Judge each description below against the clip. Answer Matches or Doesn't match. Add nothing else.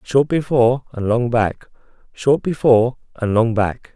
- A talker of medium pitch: Doesn't match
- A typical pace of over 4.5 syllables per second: Doesn't match